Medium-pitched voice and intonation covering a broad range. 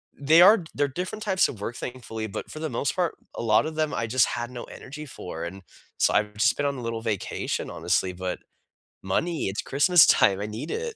No: low, 125 Hz; wide, 6.7 semitones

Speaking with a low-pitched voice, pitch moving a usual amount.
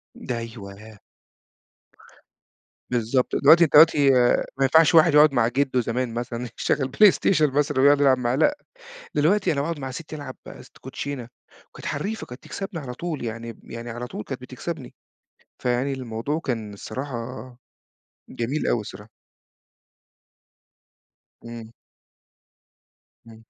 Yes: low, 130 Hz; average, 4.0 semitones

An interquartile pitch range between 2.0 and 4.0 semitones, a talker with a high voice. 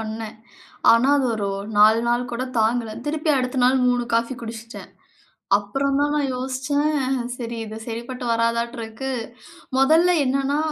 Yes: average, 2.9 semitones; very high, 250 Hz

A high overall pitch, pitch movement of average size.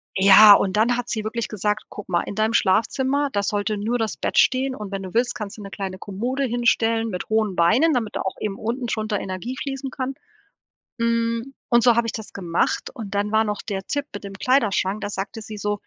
Yes: high, 215 Hz; average, 3.0 semitones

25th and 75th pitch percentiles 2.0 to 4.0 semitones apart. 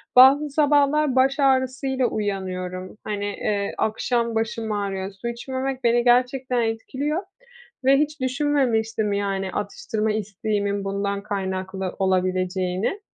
No: average, 4.8 semitones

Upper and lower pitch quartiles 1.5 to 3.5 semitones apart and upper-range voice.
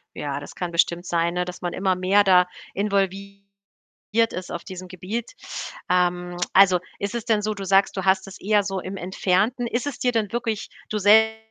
Yes: average, 2.7 semitones; high, 195 Hz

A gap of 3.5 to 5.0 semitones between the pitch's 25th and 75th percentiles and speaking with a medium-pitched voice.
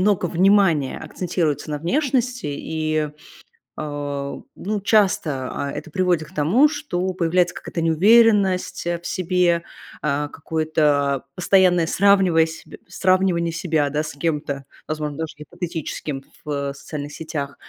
Yes: average, 3.9 semitones; medium, 165 Hz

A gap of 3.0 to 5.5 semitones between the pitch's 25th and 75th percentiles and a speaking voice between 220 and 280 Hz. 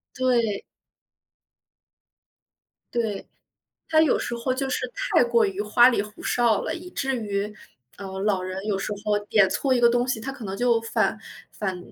Yes: average, 3.6 semitones; high, 225 Hz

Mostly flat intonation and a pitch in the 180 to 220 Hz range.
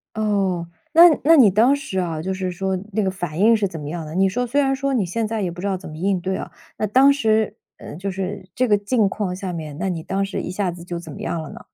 No: average, 3.6 semitones; high, 195 Hz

